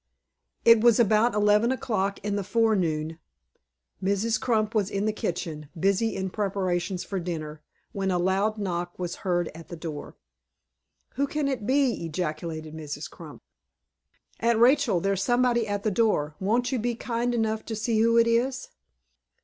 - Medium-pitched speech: No, high, 205 Hz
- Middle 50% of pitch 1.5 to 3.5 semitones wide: No, average, 4.6 semitones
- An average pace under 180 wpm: Yes, average, 160 wpm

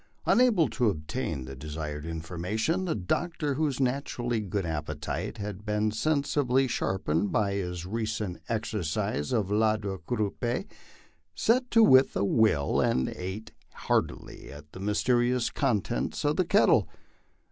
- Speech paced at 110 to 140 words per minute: Yes, slow, 135 wpm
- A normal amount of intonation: No, wide, 6.5 semitones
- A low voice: Yes, low, 105 Hz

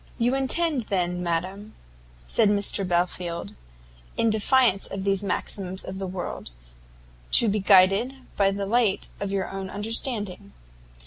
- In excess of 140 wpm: No, slow, 135 wpm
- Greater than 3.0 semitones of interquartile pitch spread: No, average, 2.7 semitones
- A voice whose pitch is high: Yes, high, 195 Hz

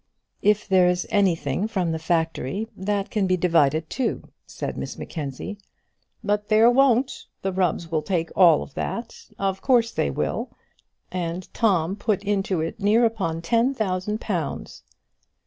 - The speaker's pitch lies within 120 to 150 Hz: No, high, 190 Hz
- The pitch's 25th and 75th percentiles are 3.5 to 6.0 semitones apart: Yes, average, 4.2 semitones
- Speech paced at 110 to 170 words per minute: Yes, average, 145 wpm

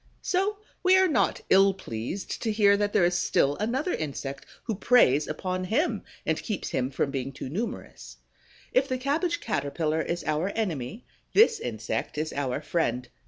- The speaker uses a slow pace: No, average, 165 wpm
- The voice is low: No, high, 190 Hz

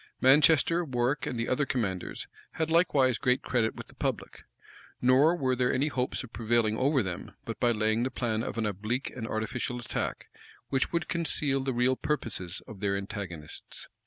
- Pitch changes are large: No, average, 3.6 semitones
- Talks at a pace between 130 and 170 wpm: No, average, 180 wpm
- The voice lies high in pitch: No, low, 125 Hz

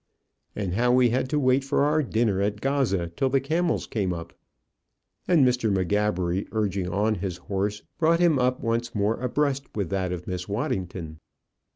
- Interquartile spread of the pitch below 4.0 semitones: No, wide, 5.5 semitones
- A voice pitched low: Yes, low, 110 Hz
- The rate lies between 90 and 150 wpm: No, average, 175 wpm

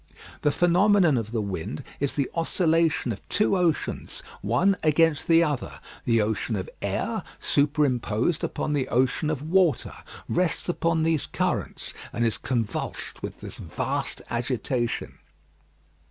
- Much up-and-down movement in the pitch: Yes, wide, 5.8 semitones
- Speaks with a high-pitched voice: No, medium, 145 Hz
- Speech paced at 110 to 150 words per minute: Yes, slow, 135 wpm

